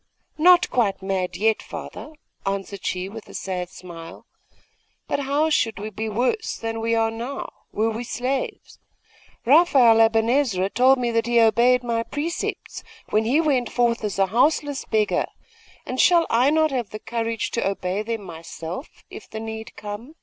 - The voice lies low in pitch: No, high, 230 Hz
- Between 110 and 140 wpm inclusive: No, average, 165 wpm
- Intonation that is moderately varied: Yes, average, 3.7 semitones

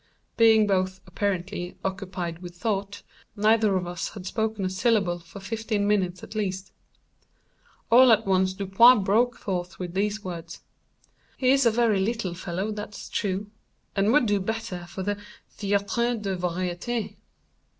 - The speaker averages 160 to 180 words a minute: No, average, 150 wpm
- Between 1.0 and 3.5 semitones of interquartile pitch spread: Yes, average, 2.8 semitones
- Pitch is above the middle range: Yes, high, 200 Hz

